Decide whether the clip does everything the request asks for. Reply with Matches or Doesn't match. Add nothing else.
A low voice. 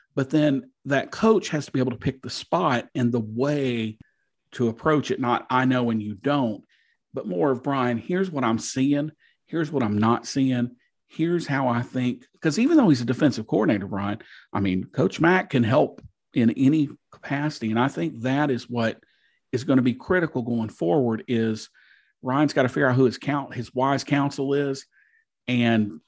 Matches